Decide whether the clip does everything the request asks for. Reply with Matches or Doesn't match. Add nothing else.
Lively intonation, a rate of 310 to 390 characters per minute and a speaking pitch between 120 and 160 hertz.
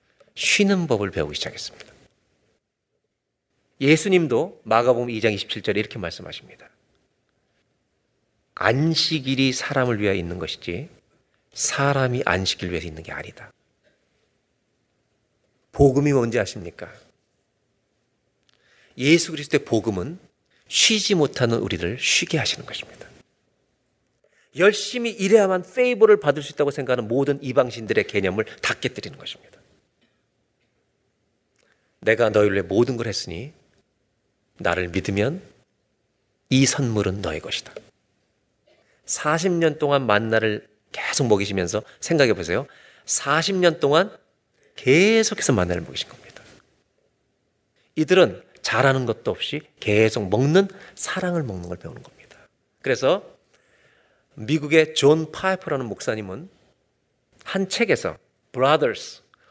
Doesn't match